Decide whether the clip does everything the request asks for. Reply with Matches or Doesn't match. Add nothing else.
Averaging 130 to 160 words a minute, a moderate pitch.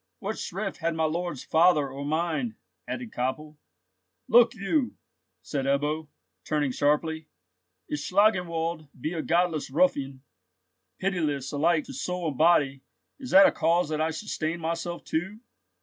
Matches